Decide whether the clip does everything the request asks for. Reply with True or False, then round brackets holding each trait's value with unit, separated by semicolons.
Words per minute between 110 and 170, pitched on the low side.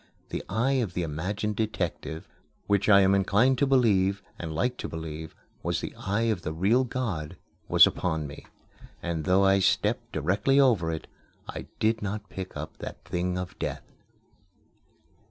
True (165 wpm; 95 Hz)